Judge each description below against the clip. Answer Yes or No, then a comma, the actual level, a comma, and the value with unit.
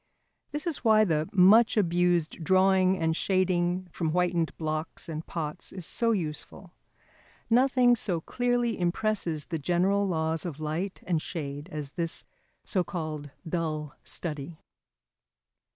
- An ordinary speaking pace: No, slow, 130 wpm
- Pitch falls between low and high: Yes, medium, 175 Hz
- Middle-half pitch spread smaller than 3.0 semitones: No, average, 3.5 semitones